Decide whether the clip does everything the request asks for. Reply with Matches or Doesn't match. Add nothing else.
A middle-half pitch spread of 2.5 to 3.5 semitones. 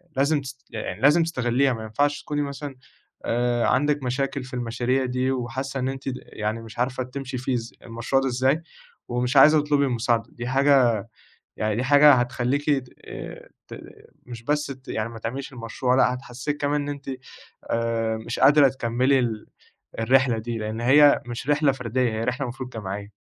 Matches